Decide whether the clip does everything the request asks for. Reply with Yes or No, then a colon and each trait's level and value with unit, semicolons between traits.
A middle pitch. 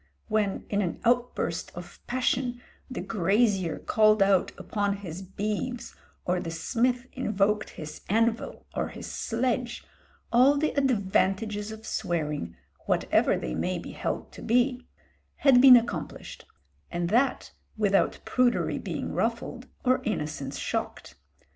No: high, 215 Hz